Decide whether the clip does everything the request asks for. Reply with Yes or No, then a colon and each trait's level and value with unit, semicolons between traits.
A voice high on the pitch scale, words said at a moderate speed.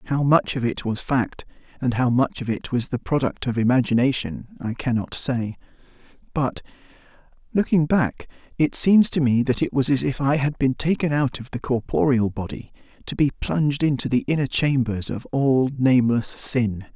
No: low, 130 Hz; average, 180 wpm